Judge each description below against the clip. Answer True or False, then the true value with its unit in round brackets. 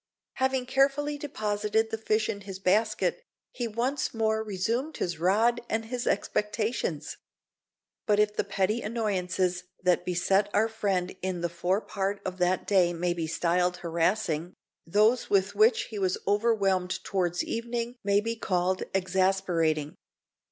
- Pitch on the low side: False (200 Hz)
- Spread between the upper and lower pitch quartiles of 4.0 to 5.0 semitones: False (3.6 semitones)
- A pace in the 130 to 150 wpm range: True (145 wpm)